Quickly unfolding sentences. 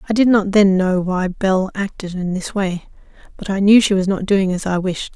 Yes: fast, 245 wpm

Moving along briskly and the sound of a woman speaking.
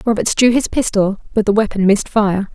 Yes: fast, 210 wpm; female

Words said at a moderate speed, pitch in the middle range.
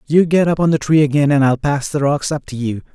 No: fast, 305 wpm; medium, 145 Hz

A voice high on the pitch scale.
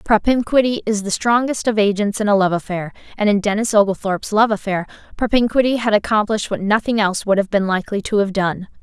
Yes: high, 210 Hz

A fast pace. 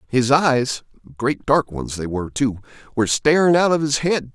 No: average, 165 wpm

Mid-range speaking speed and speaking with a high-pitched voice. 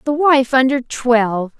Yes: average, 150 wpm; very high, 260 Hz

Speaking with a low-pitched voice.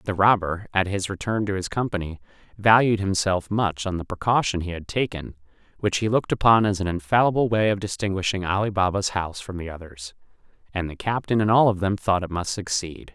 Yes: low, 100 Hz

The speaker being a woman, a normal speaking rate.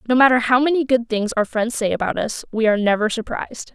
No: female; fast, 240 wpm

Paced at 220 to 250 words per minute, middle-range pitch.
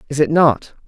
No: fast, 205 wpm; medium, 145 Hz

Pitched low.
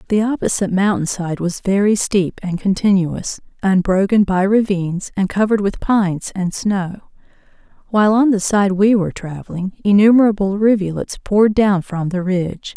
No: high, 195 Hz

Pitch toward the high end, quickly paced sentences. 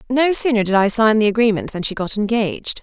Yes: high, 215 Hz; fast, 235 wpm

